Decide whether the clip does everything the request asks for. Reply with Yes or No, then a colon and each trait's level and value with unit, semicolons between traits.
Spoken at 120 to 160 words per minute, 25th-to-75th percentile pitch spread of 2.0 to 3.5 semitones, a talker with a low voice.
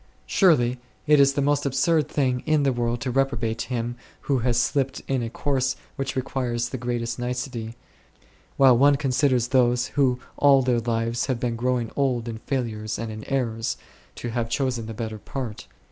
No: average, 175 wpm; narrow, 2.5 semitones; low, 125 Hz